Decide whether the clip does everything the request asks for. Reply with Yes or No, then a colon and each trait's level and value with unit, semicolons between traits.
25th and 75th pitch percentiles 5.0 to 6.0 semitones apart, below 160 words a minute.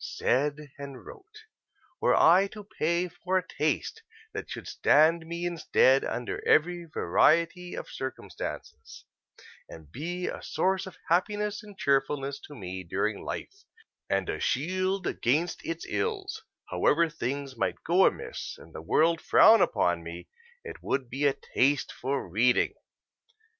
Yes: wide, 5.4 semitones; average, 145 wpm